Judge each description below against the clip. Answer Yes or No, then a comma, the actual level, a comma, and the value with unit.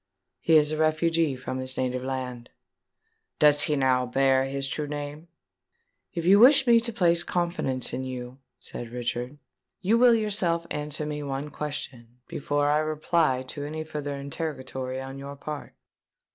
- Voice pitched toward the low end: No, medium, 145 Hz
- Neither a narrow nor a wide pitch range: Yes, average, 3.4 semitones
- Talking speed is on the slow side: No, average, 160 wpm